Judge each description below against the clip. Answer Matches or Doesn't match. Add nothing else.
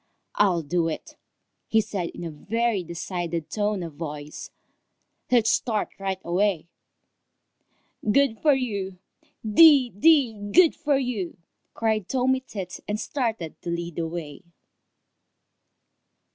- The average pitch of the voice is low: Doesn't match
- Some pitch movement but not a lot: Doesn't match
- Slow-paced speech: Matches